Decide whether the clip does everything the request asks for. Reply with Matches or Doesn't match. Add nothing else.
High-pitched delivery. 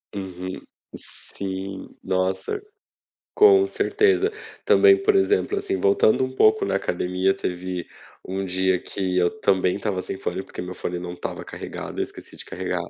Doesn't match